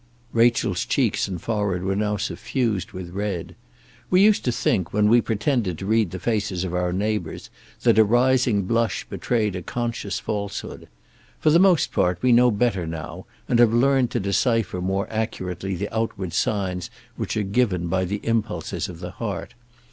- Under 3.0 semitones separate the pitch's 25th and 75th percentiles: No, average, 4.0 semitones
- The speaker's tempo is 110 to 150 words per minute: No, average, 175 wpm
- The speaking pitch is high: No, low, 105 Hz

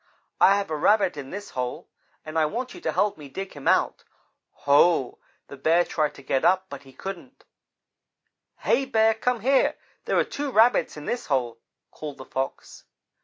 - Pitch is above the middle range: No, medium, 170 Hz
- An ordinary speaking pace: Yes, average, 185 wpm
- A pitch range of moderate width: No, wide, 7.7 semitones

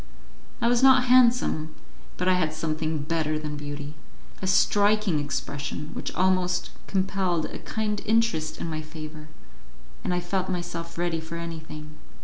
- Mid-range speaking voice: Yes, medium, 170 Hz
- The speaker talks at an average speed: Yes, average, 145 wpm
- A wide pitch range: No, average, 3.7 semitones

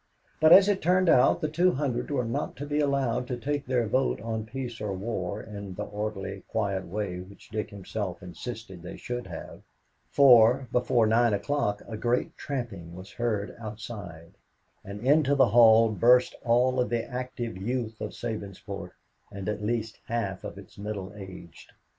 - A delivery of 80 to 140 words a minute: No, average, 170 wpm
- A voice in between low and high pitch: No, low, 115 Hz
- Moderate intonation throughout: Yes, average, 3.8 semitones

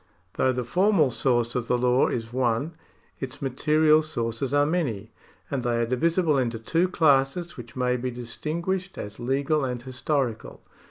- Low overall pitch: Yes, low, 130 Hz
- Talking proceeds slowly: No, average, 160 wpm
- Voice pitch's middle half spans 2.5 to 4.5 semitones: Yes, average, 4.2 semitones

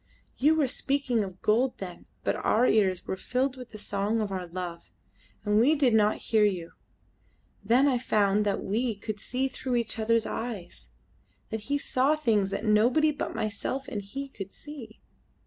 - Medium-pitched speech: No, high, 220 Hz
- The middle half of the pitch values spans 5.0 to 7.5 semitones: No, average, 4.2 semitones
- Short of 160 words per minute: No, average, 180 wpm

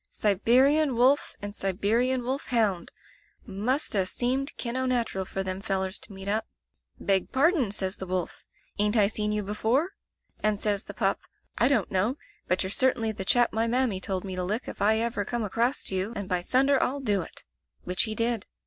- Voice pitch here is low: No, high, 215 Hz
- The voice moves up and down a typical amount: Yes, average, 4.3 semitones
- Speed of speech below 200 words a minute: No, fast, 205 wpm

